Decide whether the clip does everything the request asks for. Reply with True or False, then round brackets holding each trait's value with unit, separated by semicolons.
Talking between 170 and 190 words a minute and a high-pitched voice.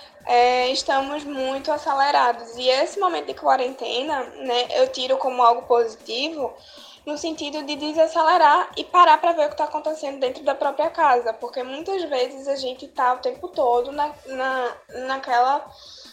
False (160 wpm; 270 Hz)